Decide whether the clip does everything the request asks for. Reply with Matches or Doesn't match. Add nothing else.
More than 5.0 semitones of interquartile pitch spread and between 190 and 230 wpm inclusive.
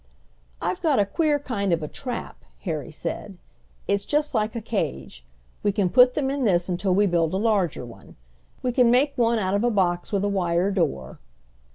Matches